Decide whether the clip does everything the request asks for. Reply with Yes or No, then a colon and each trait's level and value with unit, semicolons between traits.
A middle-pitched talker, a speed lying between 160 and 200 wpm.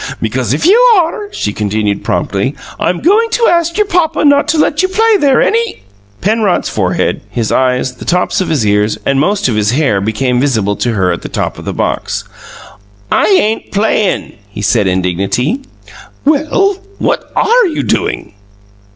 Yes: medium, 150 Hz; average, 175 wpm